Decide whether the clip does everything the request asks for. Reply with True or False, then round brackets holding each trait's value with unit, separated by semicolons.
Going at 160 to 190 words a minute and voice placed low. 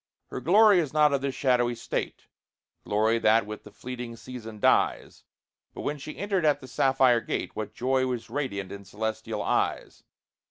True (170 wpm; 125 Hz)